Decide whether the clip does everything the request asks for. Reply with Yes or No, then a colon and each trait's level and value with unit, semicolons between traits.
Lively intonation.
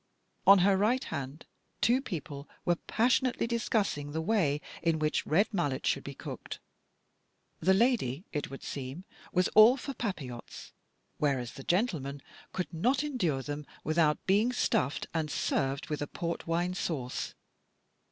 Yes: wide, 6.8 semitones